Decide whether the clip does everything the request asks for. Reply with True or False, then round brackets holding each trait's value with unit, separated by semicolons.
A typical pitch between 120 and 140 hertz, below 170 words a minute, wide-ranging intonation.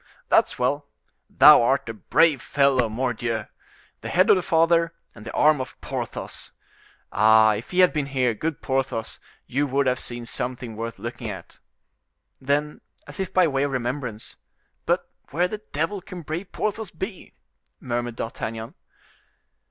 True (135 Hz; 160 wpm; 5.7 semitones)